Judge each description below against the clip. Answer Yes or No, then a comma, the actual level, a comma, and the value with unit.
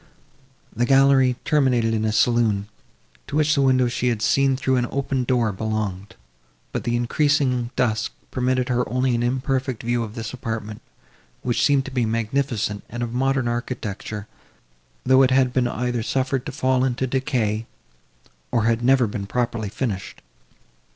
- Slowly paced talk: No, average, 160 wpm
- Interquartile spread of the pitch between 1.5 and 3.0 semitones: Yes, narrow, 2.6 semitones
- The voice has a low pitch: Yes, low, 125 Hz